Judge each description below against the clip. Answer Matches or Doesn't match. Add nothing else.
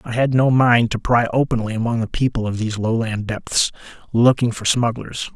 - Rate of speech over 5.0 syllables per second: Matches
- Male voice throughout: Matches